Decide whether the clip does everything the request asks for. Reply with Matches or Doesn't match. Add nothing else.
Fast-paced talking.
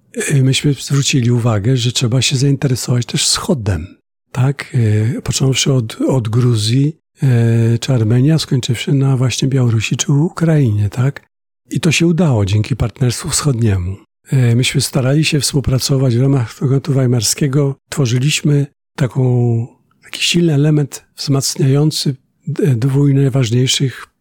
Doesn't match